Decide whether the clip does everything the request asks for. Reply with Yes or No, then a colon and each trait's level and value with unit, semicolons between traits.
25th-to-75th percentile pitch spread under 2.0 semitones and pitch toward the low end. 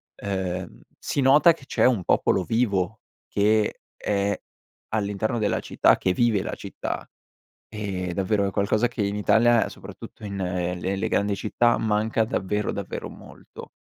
No: narrow, 2.5 semitones; low, 105 Hz